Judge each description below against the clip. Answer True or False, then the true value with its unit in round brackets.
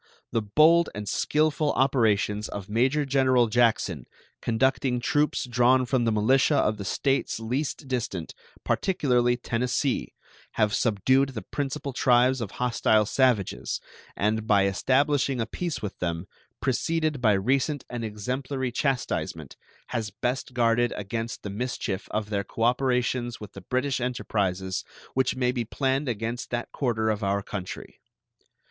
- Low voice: True (120 Hz)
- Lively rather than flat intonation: False (3.6 semitones)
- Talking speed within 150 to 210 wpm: False (140 wpm)